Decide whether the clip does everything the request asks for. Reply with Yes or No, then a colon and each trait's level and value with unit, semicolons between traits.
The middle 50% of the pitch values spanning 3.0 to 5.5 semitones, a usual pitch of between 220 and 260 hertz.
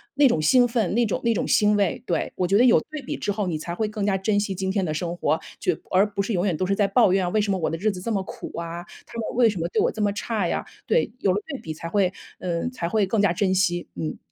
No: average, 3.5 semitones; high, 195 Hz